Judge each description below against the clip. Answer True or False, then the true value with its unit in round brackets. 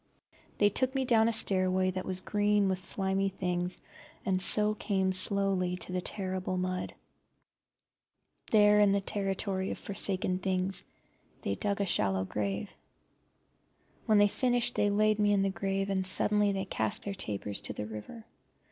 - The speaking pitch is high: True (195 Hz)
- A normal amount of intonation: False (1.9 semitones)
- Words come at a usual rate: True (165 wpm)